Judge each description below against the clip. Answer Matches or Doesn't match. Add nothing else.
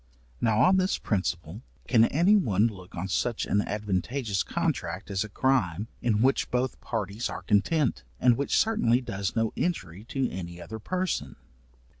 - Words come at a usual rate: Matches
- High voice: Doesn't match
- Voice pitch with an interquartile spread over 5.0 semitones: Matches